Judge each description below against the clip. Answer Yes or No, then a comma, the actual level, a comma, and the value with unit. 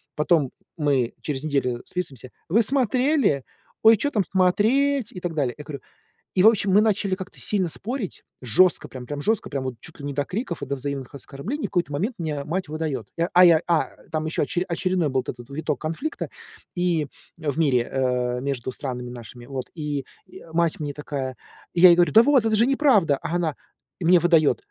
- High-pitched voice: No, medium, 160 Hz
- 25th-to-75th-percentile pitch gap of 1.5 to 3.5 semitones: No, wide, 5.4 semitones